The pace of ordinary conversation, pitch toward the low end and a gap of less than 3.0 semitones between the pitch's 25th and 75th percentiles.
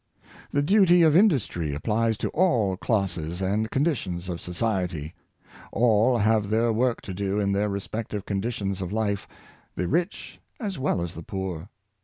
No: average, 165 wpm; low, 105 Hz; average, 4.2 semitones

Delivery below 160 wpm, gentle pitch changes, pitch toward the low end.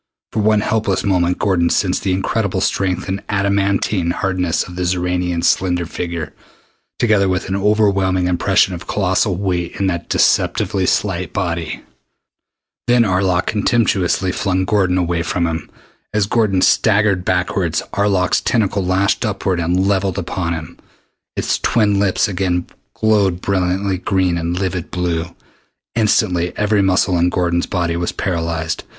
Yes: average, 140 wpm; narrow, 2.1 semitones; very low, 95 Hz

